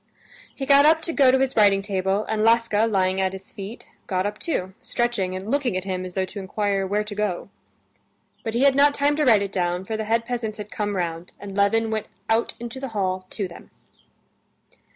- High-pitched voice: Yes, high, 210 Hz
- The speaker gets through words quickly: Yes, fast, 220 wpm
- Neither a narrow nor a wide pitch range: Yes, average, 3.7 semitones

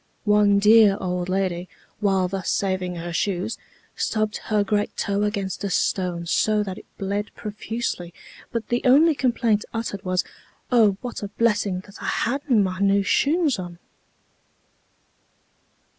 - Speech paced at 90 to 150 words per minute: Yes, average, 145 wpm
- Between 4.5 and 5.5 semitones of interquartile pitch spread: No, average, 2.9 semitones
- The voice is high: Yes, high, 205 Hz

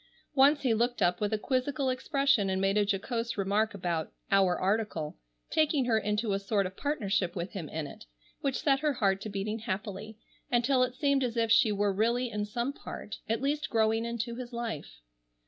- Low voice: No, high, 220 Hz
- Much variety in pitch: No, average, 4.3 semitones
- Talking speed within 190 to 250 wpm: Yes, average, 200 wpm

